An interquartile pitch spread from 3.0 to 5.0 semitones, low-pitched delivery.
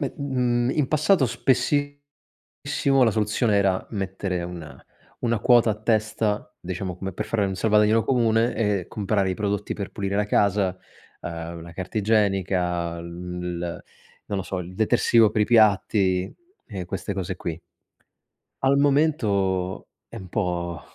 Yes: average, 3.8 semitones; low, 100 Hz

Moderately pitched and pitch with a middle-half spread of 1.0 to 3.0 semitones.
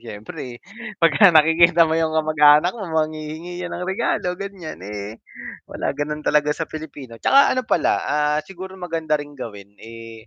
No: medium, 155 Hz; average, 3.5 semitones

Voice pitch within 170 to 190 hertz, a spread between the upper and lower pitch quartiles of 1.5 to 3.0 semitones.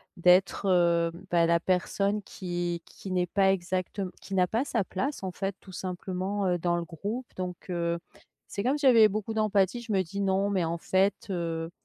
Yes: medium, 185 Hz; narrow, 2.4 semitones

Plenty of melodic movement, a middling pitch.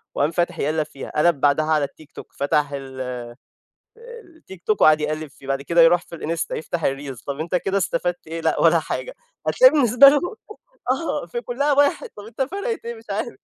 Yes: wide, 8.0 semitones; medium, 165 Hz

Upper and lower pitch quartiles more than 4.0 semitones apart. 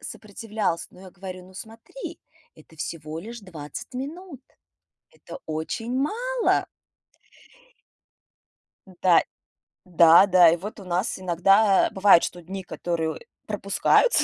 Yes: average, 4.7 semitones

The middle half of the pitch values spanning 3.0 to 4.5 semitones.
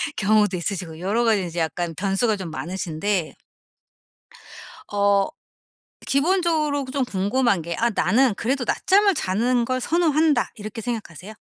No: wide, 5.6 semitones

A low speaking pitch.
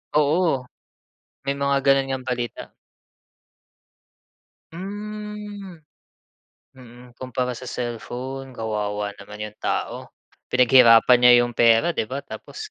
Yes: low, 130 Hz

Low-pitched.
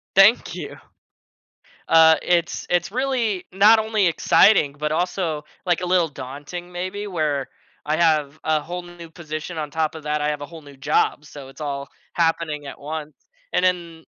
No: medium, 160 Hz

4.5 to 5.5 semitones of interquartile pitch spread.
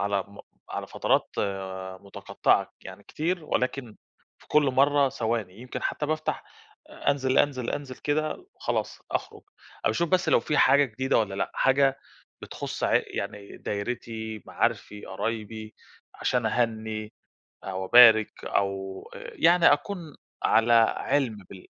Yes: average, 5.0 semitones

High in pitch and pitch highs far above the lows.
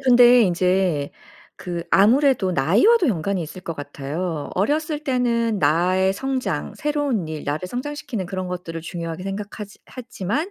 Yes: high, 195 Hz; wide, 6.6 semitones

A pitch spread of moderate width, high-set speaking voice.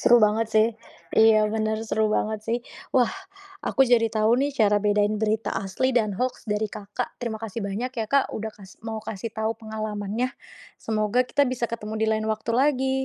No: narrow, 2.0 semitones; high, 220 Hz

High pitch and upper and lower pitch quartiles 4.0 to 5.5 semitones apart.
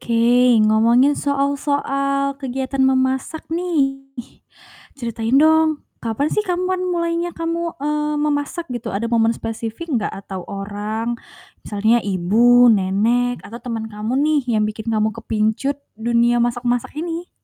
Yes: high, 245 Hz; average, 4.5 semitones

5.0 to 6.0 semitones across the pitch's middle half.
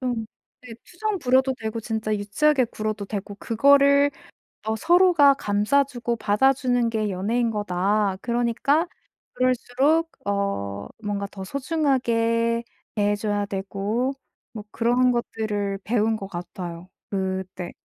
No: average, 4.0 semitones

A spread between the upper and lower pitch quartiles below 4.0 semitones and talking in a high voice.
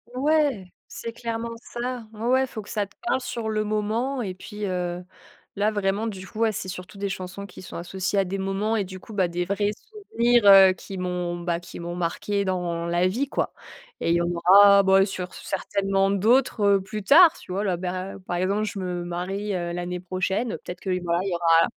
Yes: average, 3.0 semitones; high, 195 Hz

